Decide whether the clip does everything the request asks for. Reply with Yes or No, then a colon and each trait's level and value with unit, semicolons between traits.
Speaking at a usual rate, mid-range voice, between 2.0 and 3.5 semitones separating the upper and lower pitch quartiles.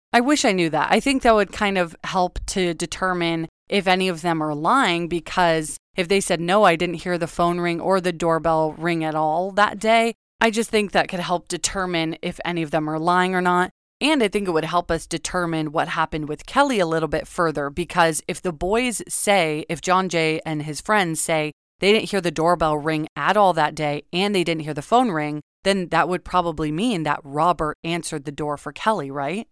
No: fast, 230 wpm; medium, 175 Hz; average, 2.9 semitones